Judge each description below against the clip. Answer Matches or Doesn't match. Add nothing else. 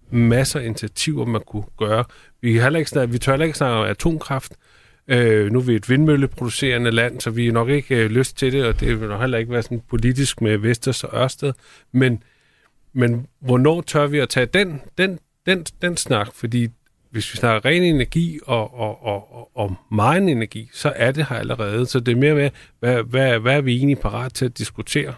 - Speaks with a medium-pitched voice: Doesn't match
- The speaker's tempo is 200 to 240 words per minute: Matches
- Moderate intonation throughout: Matches